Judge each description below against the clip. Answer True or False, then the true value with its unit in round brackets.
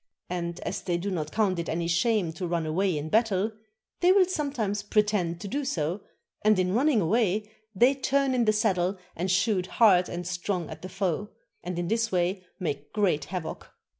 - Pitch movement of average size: True (4.0 semitones)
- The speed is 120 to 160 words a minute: False (195 wpm)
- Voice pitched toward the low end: False (190 Hz)